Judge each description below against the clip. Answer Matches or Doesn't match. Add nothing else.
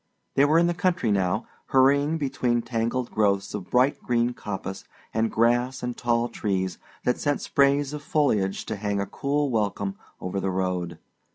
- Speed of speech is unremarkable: Matches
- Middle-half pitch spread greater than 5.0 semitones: Matches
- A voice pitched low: Matches